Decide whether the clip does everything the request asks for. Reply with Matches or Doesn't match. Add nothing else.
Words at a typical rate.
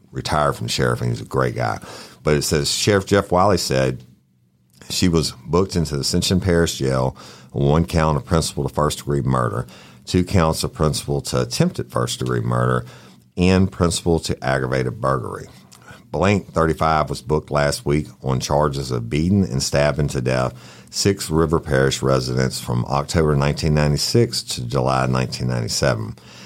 Matches